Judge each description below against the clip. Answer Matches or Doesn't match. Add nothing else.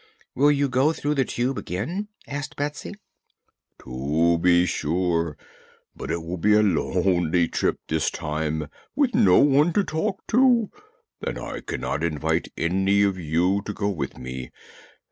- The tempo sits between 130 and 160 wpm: Matches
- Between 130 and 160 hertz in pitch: Doesn't match